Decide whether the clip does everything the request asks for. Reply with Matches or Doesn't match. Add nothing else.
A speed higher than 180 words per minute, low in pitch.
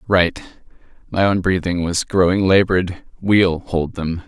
Doesn't match